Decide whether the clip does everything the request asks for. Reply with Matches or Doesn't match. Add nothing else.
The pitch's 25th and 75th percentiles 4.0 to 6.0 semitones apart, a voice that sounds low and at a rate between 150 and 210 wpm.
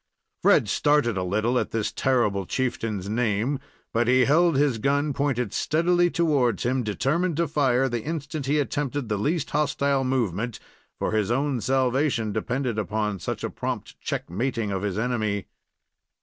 Matches